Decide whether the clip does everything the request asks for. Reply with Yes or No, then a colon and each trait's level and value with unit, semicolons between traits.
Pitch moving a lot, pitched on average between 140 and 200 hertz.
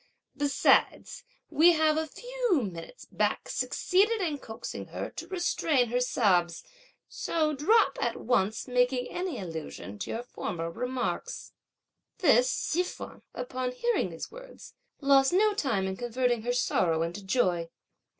No: wide, 8.0 semitones; very high, 255 Hz